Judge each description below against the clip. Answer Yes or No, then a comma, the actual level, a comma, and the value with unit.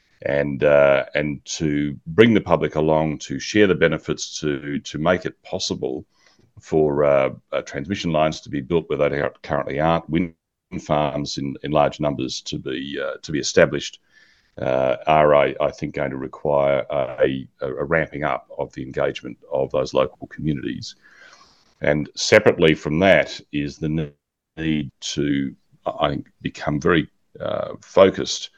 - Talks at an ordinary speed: Yes, average, 155 wpm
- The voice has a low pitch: Yes, very low, 75 Hz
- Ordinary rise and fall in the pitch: No, narrow, 1.9 semitones